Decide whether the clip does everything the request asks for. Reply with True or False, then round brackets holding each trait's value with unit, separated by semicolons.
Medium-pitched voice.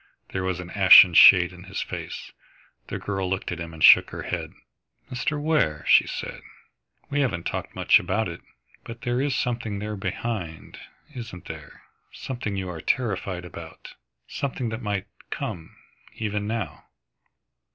False (100 Hz)